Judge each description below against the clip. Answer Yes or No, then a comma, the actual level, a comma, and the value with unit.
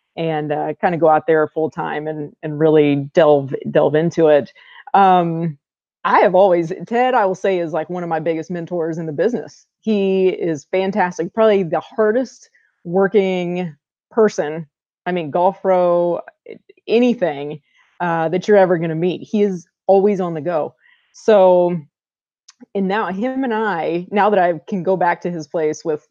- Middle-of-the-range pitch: Yes, medium, 175 Hz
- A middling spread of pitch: Yes, average, 3.7 semitones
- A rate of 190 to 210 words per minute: No, average, 175 wpm